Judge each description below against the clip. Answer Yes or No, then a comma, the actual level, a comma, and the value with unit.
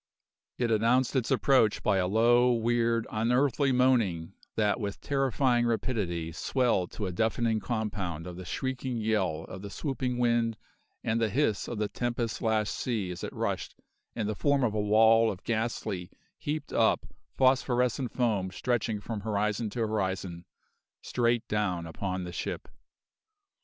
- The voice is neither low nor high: No, low, 110 Hz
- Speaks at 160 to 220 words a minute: No, average, 150 wpm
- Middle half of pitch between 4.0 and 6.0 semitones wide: No, average, 3.4 semitones